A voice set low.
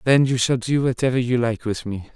Yes: low, 120 Hz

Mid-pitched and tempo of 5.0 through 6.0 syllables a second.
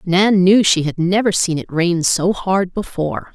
No: medium, 180 Hz; 4.3 syllables/s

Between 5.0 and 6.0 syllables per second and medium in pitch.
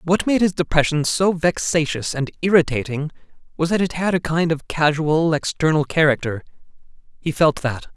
Yes: 5.1 syllables/s; medium, 160 Hz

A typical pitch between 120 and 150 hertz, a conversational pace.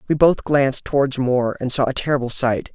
No: low, 135 Hz; fast, 220 wpm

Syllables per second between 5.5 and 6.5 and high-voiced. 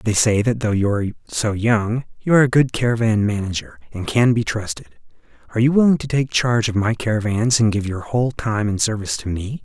No: 6.0 syllables/s; low, 110 Hz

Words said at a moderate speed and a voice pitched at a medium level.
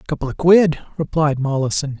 Yes: average, 150 wpm; medium, 150 Hz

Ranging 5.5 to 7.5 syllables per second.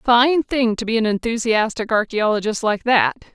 No: 4.6 syllables/s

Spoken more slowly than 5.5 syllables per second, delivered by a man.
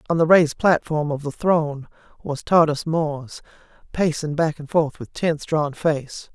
No: 4.5 syllables/s; female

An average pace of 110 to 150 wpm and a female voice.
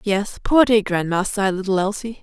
No: average, 190 wpm; female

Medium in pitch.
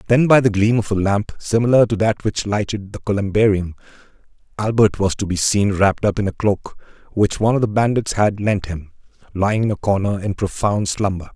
No: low, 105 Hz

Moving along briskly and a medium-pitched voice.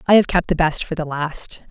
Yes: fast, 280 wpm; medium, 165 Hz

